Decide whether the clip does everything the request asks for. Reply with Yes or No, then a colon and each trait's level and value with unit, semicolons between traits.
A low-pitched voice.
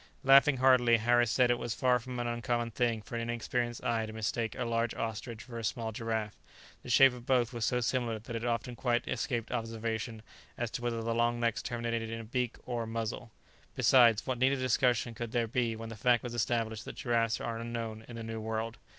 Yes: low, 115 Hz